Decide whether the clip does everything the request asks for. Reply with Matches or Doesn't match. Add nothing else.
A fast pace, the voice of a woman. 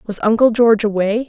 Doesn't match